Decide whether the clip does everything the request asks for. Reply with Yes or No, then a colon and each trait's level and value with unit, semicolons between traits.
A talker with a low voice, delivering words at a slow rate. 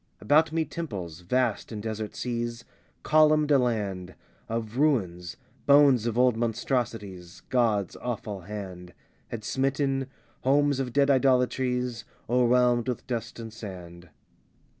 Yes: low, 120 Hz; slow, 120 wpm